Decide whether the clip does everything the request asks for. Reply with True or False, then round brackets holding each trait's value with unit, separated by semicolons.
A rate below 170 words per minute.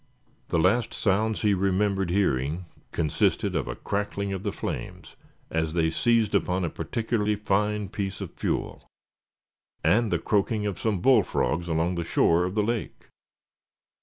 True (150 wpm)